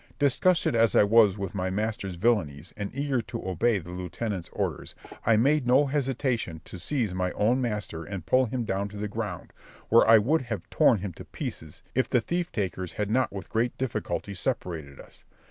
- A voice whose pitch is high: No, low, 105 Hz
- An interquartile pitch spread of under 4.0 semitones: No, average, 5.0 semitones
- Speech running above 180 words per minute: Yes, average, 195 wpm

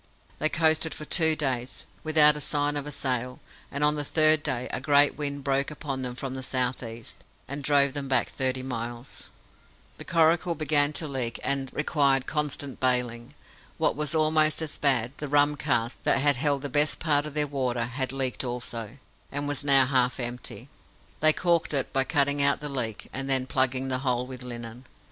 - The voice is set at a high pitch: No, medium, 140 Hz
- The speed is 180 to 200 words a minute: Yes, average, 190 wpm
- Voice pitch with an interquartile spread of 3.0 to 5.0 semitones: No, narrow, 2.6 semitones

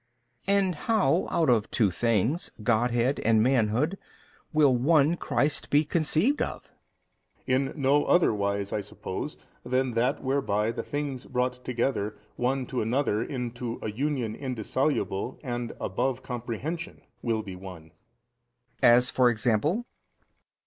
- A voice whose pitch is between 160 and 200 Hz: No, low, 125 Hz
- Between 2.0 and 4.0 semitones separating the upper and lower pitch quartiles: No, average, 4.4 semitones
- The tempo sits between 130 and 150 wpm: Yes, slow, 135 wpm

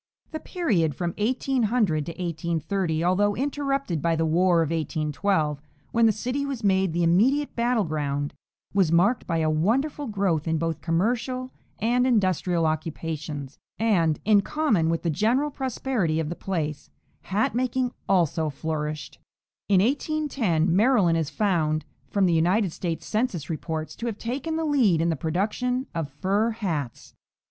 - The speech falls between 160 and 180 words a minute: No, average, 150 wpm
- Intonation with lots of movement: Yes, wide, 6.6 semitones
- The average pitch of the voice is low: No, medium, 185 Hz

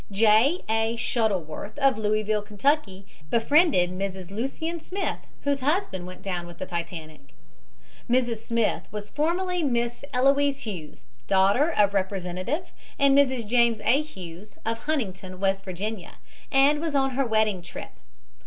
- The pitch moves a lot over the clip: Yes, wide, 6.3 semitones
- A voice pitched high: Yes, high, 220 Hz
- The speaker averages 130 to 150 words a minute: Yes, slow, 135 wpm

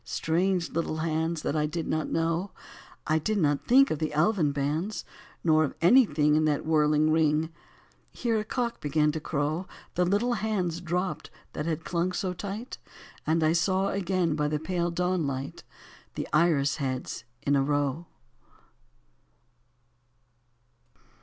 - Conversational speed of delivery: Yes, average, 155 wpm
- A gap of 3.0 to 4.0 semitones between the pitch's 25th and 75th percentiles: Yes, average, 3.3 semitones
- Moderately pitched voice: Yes, medium, 160 Hz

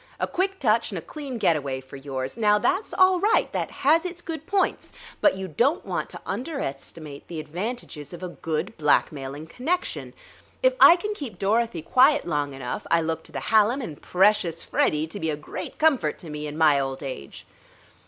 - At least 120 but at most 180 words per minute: No, average, 190 wpm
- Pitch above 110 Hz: Yes, medium, 185 Hz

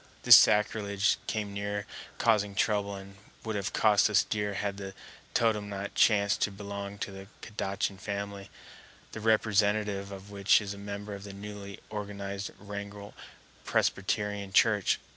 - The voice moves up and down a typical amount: No, narrow, 0.8 semitones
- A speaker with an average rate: Yes, average, 145 wpm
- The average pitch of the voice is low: Yes, low, 100 Hz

